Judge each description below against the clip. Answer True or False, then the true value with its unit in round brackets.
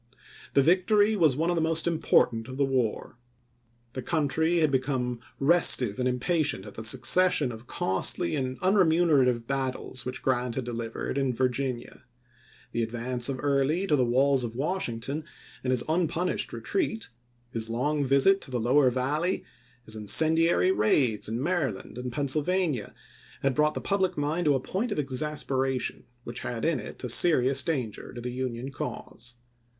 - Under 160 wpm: False (165 wpm)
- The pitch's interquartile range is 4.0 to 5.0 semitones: True (4.6 semitones)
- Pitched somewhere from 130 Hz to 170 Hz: True (135 Hz)